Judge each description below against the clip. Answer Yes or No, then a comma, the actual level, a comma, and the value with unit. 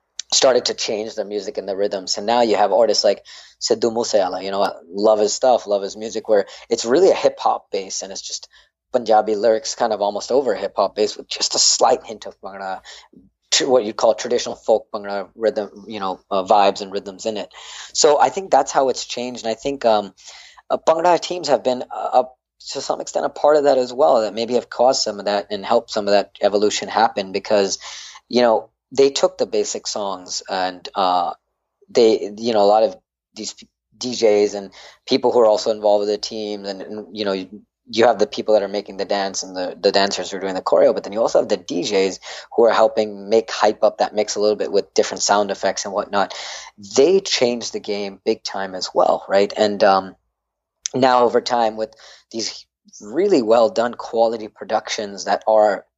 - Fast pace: Yes, fast, 220 wpm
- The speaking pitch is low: Yes, low, 110 Hz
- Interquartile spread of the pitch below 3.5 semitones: No, average, 3.8 semitones